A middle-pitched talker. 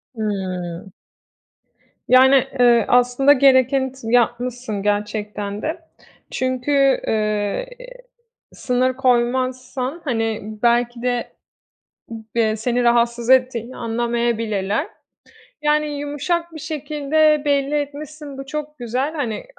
No: very high, 250 Hz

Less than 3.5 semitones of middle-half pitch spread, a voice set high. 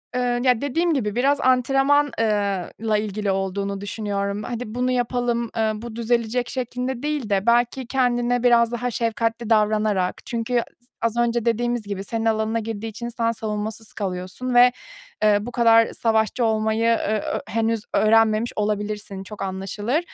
Yes: narrow, 2.4 semitones; high, 225 Hz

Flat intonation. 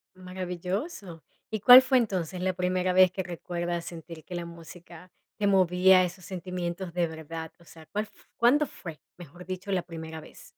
Yes: narrow, 1.8 semitones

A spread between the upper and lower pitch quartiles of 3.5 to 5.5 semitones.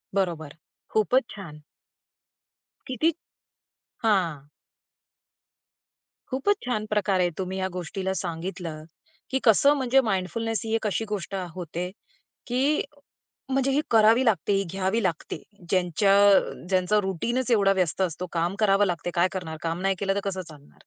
Yes: average, 3.9 semitones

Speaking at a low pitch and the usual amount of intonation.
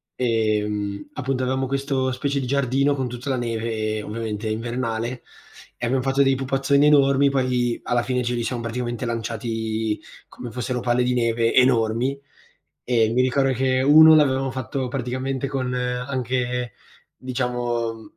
No: low, 125 Hz; narrow, 2.3 semitones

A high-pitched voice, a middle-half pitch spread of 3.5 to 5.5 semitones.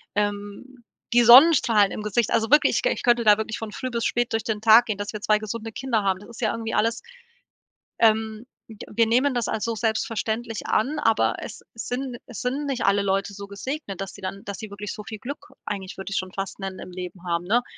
No: high, 220 Hz; average, 2.9 semitones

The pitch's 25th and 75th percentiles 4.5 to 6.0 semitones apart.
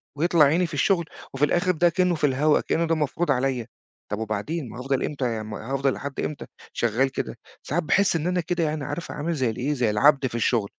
Yes: average, 4.8 semitones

